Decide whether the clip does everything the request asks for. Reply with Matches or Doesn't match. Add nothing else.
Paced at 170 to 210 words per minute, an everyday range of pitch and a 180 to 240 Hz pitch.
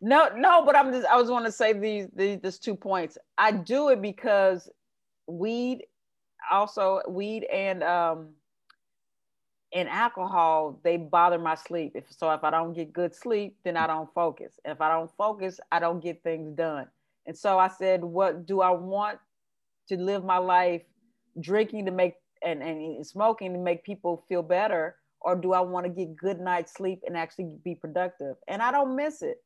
Matches